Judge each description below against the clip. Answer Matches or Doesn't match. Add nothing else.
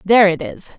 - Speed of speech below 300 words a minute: Matches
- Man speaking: Doesn't match